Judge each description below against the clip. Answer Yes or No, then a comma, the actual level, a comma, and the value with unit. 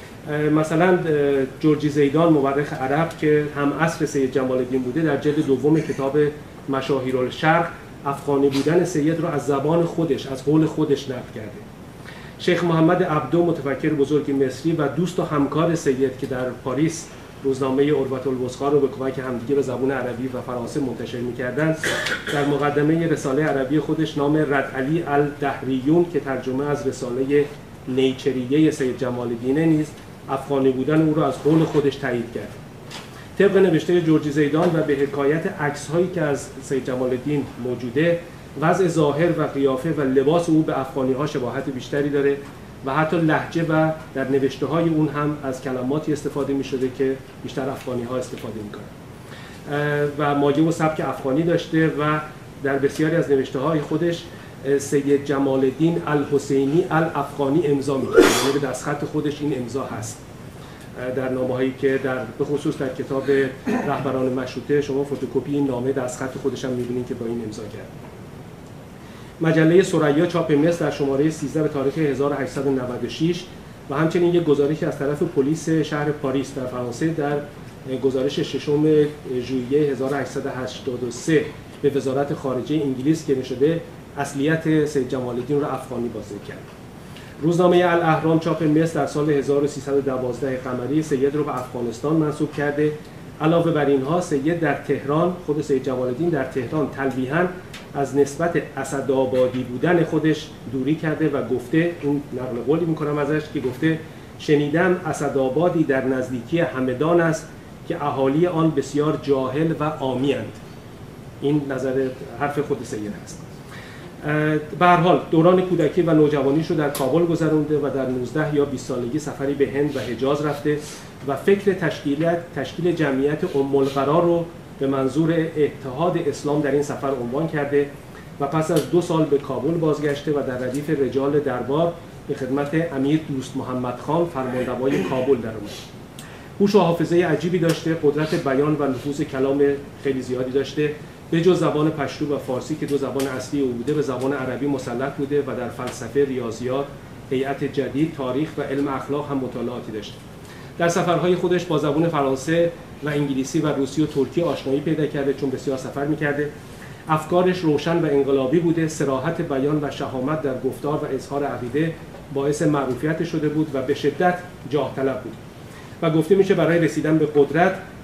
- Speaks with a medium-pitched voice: Yes, medium, 145 Hz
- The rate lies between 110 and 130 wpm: No, fast, 155 wpm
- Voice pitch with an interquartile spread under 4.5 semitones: Yes, average, 2.7 semitones